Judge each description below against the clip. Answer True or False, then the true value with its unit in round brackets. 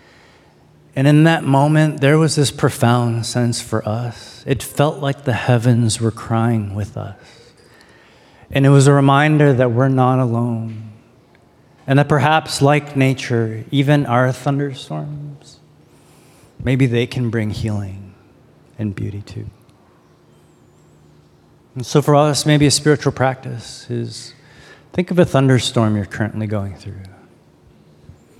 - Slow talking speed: True (130 wpm)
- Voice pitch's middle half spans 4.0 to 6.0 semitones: True (4.5 semitones)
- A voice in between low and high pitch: False (125 Hz)